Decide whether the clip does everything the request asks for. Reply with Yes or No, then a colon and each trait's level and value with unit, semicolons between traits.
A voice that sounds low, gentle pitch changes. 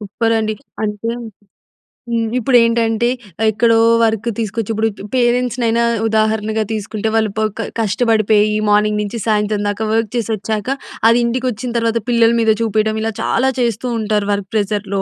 No: high, 220 Hz; narrow, 1.6 semitones